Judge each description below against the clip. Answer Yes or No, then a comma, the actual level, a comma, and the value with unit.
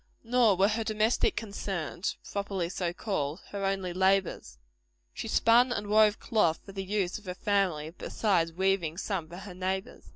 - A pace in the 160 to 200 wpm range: Yes, average, 170 wpm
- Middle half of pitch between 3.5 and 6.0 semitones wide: No, average, 2.8 semitones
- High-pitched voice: Yes, high, 195 Hz